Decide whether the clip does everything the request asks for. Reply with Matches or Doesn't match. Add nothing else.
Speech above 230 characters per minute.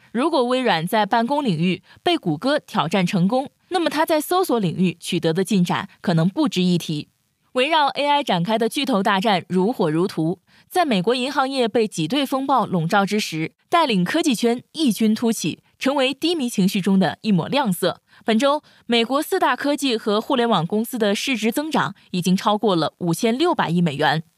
Matches